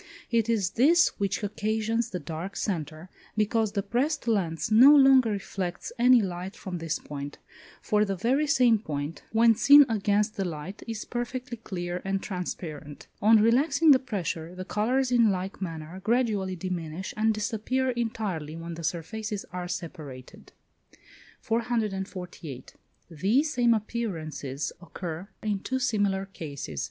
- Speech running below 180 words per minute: Yes, average, 140 wpm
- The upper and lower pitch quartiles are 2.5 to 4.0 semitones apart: No, average, 4.9 semitones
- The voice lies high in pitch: Yes, high, 205 Hz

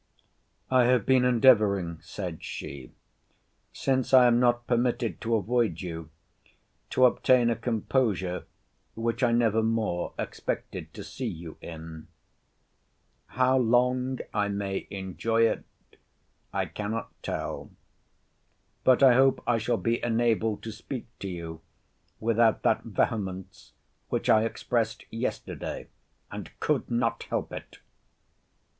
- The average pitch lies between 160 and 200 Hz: No, low, 115 Hz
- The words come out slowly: Yes, slow, 125 wpm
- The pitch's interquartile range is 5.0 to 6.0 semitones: No, average, 3.8 semitones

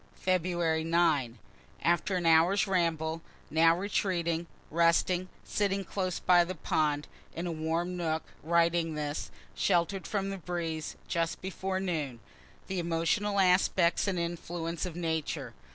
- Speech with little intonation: Yes, narrow, 2.2 semitones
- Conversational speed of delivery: No, slow, 130 wpm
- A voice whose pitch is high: No, medium, 170 Hz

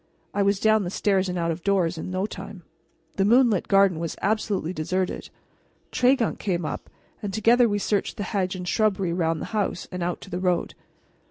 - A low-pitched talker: No, high, 195 Hz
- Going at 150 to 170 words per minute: No, average, 195 wpm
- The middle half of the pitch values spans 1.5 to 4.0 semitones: Yes, average, 2.7 semitones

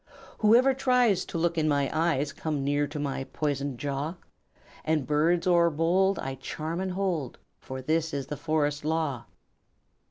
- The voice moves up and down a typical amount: Yes, average, 3.2 semitones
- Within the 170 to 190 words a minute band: No, average, 155 wpm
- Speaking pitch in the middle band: Yes, medium, 155 Hz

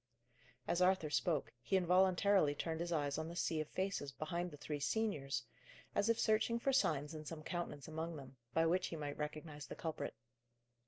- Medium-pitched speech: Yes, medium, 165 Hz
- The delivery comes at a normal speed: Yes, average, 190 wpm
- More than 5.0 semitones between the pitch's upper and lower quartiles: No, average, 3.5 semitones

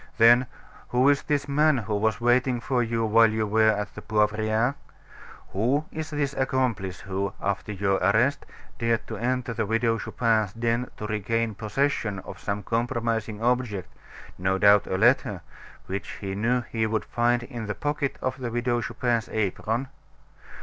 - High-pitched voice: No, low, 115 Hz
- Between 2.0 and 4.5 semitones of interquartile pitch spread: Yes, average, 2.8 semitones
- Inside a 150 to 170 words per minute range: Yes, average, 165 wpm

